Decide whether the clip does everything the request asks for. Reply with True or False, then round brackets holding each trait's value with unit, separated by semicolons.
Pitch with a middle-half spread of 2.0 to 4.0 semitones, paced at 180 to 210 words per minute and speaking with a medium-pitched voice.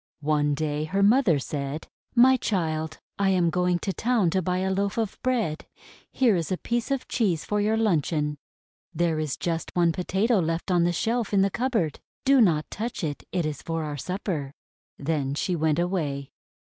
False (4.9 semitones; 190 wpm; 175 Hz)